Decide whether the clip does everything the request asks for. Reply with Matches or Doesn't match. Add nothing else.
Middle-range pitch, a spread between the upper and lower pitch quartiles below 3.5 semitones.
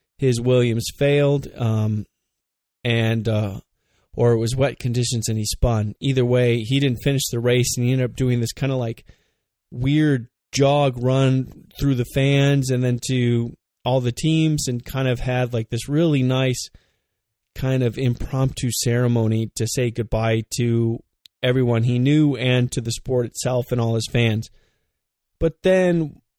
Doesn't match